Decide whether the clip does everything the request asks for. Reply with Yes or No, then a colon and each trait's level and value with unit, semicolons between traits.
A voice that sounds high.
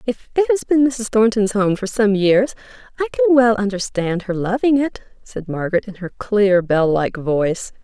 Yes: high, 210 Hz